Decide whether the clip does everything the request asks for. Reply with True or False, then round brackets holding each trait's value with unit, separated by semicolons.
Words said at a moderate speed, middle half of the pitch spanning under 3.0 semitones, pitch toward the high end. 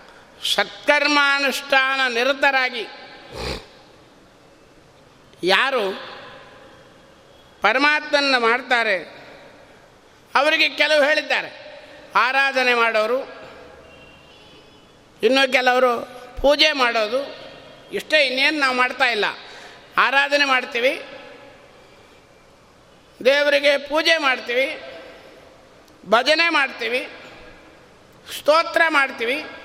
False (55 wpm; 2.5 semitones; 275 Hz)